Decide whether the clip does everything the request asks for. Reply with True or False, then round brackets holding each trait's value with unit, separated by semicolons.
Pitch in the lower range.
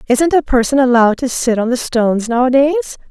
False (245 Hz)